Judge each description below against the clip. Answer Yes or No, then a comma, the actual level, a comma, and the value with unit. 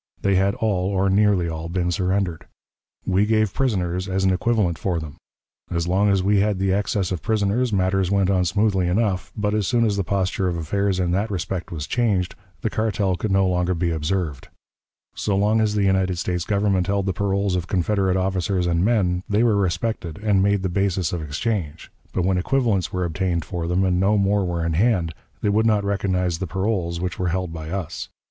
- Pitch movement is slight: Yes, narrow, 2.3 semitones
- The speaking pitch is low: Yes, very low, 95 Hz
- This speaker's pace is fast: Yes, fast, 210 wpm